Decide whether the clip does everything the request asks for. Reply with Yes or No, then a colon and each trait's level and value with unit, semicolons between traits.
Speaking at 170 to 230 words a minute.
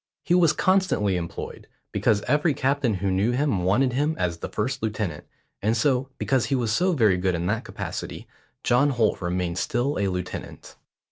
Yes: average, 180 wpm